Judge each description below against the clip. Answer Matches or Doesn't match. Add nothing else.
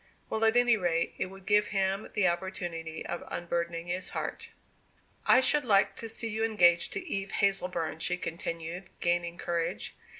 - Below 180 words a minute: Matches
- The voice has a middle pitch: Matches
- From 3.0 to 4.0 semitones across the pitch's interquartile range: Matches